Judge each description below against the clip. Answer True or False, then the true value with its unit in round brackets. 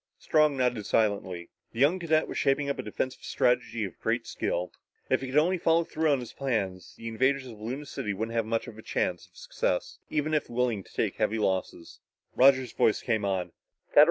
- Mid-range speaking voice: False (125 Hz)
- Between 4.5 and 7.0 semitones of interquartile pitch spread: True (4.8 semitones)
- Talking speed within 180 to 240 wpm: True (195 wpm)